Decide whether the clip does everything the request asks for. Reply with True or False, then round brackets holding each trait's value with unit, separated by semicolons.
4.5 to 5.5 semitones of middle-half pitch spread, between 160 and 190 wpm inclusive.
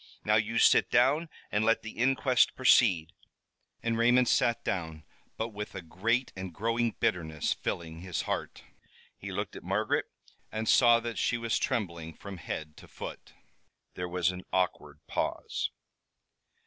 False (5.2 semitones; 150 wpm)